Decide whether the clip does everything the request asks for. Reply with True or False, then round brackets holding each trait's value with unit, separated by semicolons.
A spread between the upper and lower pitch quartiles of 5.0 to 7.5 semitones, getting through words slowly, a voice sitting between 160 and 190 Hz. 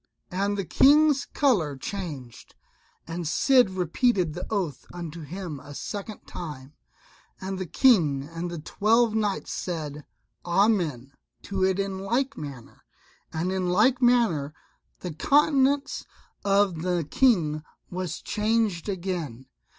True (5.3 semitones; 125 wpm; 185 Hz)